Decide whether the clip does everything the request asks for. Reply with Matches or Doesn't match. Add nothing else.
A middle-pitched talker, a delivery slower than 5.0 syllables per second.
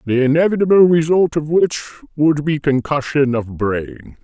Matches